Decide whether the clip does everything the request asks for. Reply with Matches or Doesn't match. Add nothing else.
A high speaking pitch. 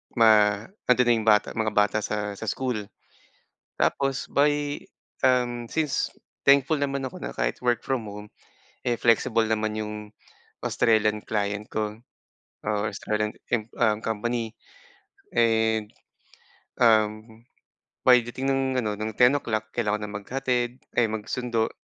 Doesn't match